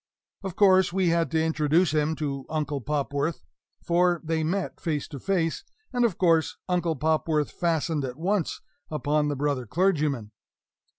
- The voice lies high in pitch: No, medium, 160 Hz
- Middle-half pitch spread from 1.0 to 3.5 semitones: Yes, average, 2.9 semitones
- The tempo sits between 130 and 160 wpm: Yes, average, 155 wpm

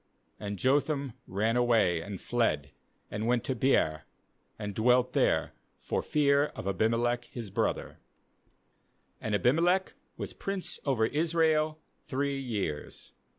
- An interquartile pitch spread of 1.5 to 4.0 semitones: No, average, 5.1 semitones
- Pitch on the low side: Yes, low, 120 Hz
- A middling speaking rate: No, slow, 120 wpm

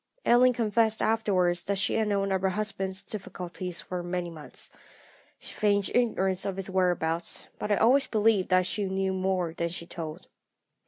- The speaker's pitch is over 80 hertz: Yes, high, 190 Hz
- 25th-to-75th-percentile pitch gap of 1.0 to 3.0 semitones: Yes, average, 2.7 semitones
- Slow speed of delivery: No, average, 170 wpm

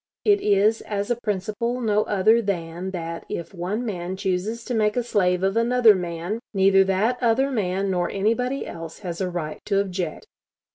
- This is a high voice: Yes, high, 200 Hz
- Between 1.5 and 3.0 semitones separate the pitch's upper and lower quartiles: No, average, 3.9 semitones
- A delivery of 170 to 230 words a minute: Yes, average, 180 wpm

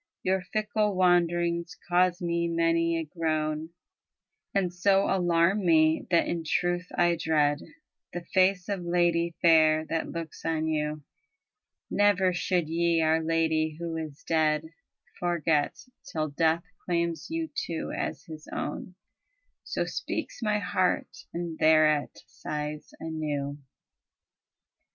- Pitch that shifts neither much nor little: No, narrow, 2.0 semitones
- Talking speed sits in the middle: No, slow, 125 wpm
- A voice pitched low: No, medium, 165 Hz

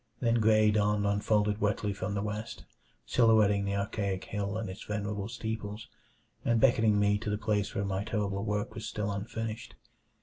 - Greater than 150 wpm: Yes, average, 170 wpm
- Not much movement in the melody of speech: Yes, narrow, 1.4 semitones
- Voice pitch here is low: Yes, low, 105 Hz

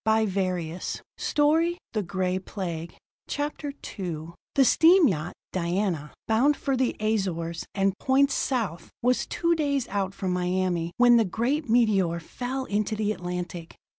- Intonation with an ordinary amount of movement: No, wide, 6.3 semitones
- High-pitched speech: Yes, high, 205 Hz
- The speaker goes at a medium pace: No, slow, 130 wpm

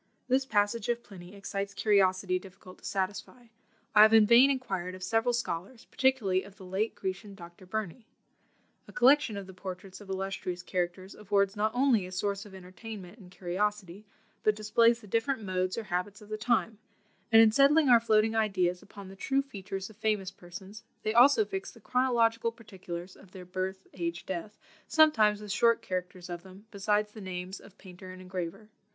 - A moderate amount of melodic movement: Yes, average, 3.2 semitones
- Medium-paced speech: Yes, average, 180 wpm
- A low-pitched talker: No, high, 200 Hz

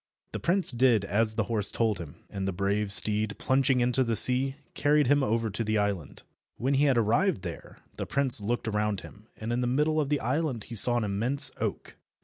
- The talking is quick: Yes, fast, 215 wpm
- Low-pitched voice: Yes, low, 115 Hz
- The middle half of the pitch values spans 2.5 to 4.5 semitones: Yes, average, 4.2 semitones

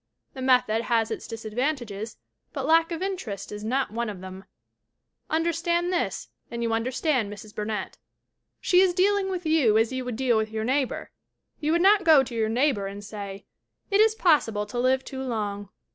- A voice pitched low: No, very high, 250 Hz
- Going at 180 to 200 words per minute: Yes, average, 185 wpm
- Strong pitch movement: Yes, wide, 6.8 semitones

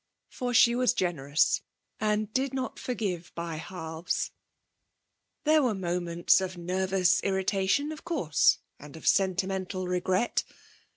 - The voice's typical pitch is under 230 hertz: Yes, high, 190 Hz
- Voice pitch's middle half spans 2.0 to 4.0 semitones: No, average, 4.6 semitones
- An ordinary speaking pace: No, slow, 120 wpm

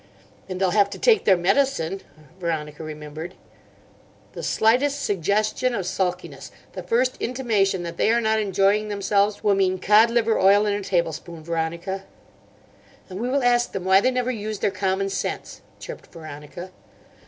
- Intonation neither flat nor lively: Yes, average, 3.7 semitones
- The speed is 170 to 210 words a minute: No, average, 155 wpm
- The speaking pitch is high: Yes, high, 195 Hz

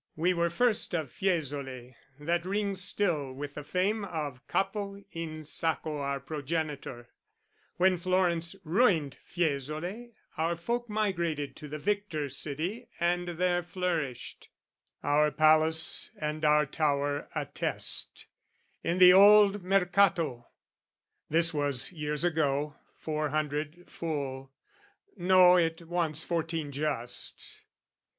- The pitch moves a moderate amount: Yes, average, 3.5 semitones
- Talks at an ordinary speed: No, slow, 115 wpm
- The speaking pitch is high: No, medium, 160 Hz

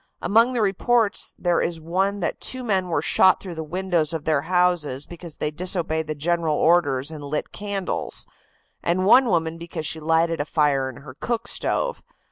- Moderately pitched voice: Yes, medium, 170 Hz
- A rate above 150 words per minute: Yes, average, 185 wpm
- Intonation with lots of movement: No, average, 3.6 semitones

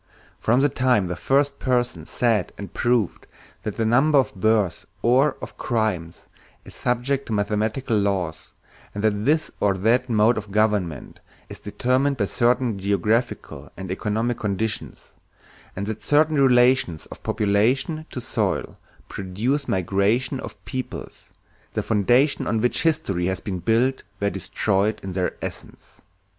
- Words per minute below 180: Yes, average, 145 wpm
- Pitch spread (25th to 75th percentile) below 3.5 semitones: No, average, 4.3 semitones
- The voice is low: Yes, low, 110 Hz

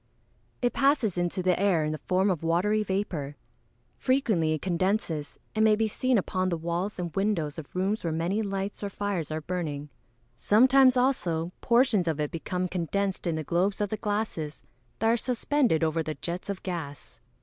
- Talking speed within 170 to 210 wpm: Yes, average, 185 wpm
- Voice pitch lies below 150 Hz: No, medium, 185 Hz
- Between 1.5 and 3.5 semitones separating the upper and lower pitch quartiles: No, average, 4.4 semitones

